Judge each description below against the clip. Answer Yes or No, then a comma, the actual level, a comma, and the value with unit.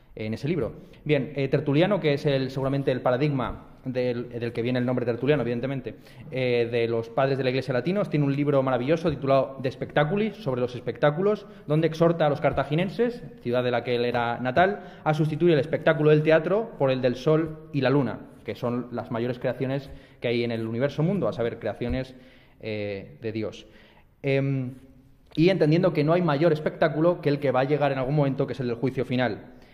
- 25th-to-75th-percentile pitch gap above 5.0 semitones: No, average, 3.8 semitones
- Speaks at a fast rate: Yes, fast, 210 wpm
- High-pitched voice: No, low, 135 Hz